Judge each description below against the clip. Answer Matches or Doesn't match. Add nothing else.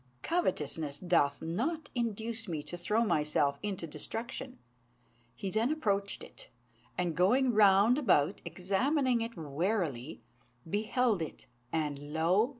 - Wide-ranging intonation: Matches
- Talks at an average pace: Doesn't match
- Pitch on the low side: Doesn't match